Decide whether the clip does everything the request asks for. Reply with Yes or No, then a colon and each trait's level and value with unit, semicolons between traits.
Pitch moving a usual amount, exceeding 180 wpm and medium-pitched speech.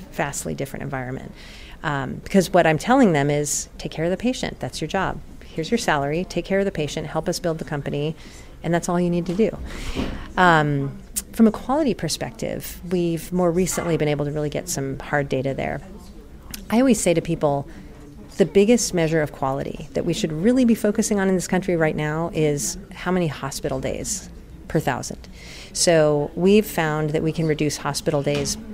Yes: average, 4.0 semitones; average, 195 wpm; medium, 170 Hz